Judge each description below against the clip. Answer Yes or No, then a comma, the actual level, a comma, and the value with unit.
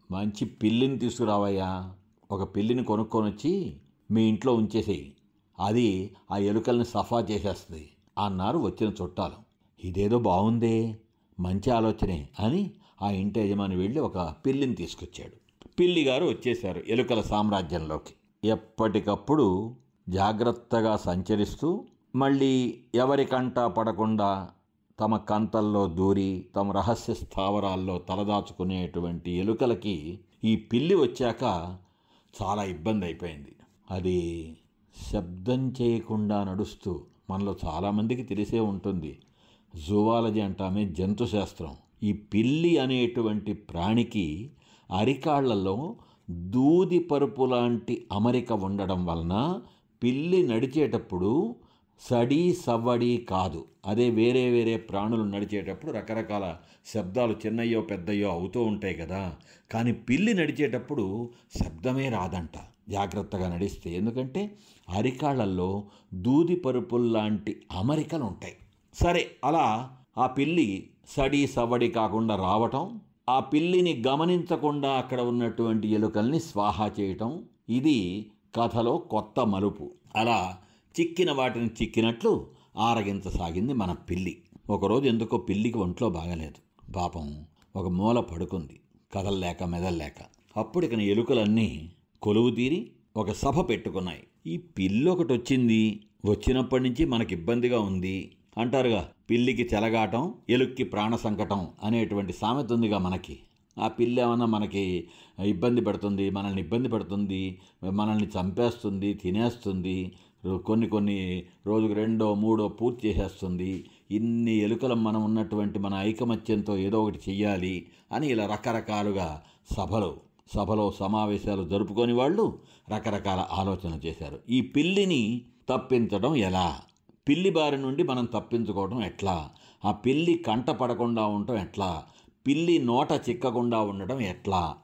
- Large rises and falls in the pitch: No, average, 3.7 semitones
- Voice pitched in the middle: No, low, 105 Hz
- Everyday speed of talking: Yes, average, 100 wpm